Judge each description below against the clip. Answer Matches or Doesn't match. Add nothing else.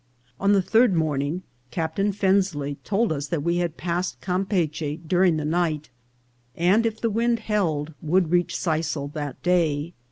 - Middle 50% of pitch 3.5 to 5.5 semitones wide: Matches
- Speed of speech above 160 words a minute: Doesn't match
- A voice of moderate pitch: Matches